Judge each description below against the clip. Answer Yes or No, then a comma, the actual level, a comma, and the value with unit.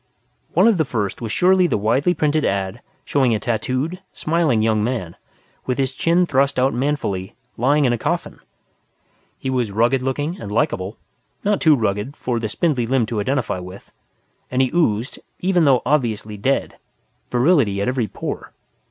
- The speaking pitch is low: Yes, low, 130 Hz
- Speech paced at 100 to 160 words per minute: No, average, 170 wpm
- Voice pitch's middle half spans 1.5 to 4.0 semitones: No, average, 5.3 semitones